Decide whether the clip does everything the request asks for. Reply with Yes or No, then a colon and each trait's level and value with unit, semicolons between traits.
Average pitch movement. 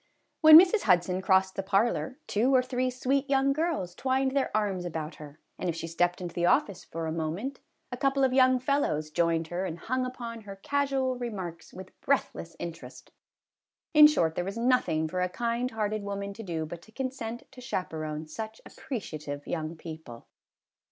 No: wide, 7.3 semitones